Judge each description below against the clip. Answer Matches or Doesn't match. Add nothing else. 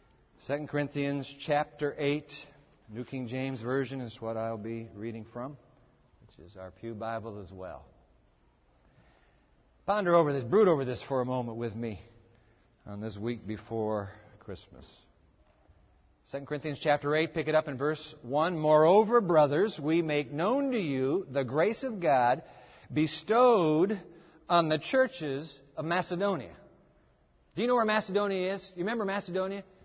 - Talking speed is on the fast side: Doesn't match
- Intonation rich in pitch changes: Matches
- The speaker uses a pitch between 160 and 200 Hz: Doesn't match